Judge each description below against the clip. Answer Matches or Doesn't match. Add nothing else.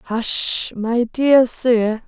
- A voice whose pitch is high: Matches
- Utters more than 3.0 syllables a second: Doesn't match